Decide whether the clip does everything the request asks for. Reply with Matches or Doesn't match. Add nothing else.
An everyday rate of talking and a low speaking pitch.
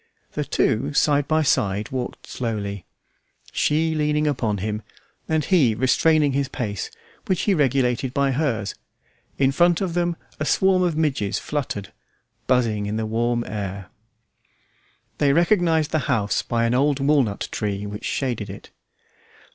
Matches